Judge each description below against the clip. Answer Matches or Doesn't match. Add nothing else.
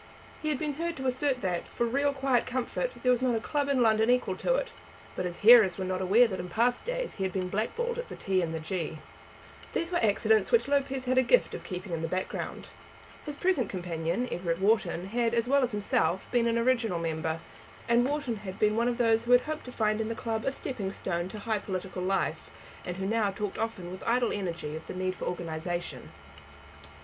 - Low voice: Doesn't match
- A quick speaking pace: Matches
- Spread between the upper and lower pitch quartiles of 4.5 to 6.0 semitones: Matches